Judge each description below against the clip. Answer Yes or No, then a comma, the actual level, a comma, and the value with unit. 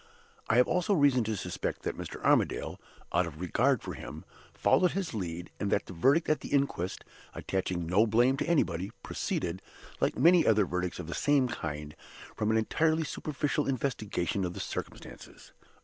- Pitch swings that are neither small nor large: No, wide, 8.1 semitones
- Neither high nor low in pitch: No, low, 110 Hz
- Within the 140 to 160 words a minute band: No, average, 175 wpm